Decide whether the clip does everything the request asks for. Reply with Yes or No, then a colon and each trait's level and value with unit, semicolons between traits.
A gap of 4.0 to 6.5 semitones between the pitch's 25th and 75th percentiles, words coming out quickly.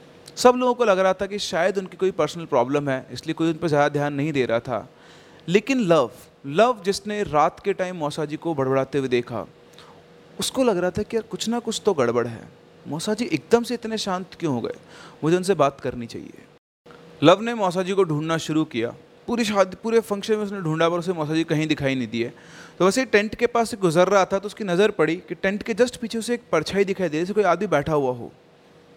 Yes: wide, 5.6 semitones; fast, 240 wpm